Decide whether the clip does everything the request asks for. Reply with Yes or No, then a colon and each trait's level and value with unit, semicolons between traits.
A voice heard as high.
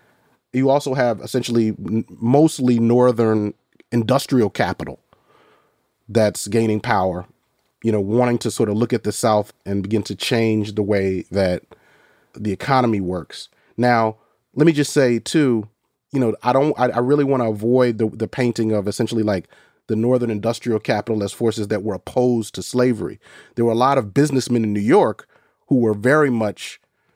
No: low, 115 Hz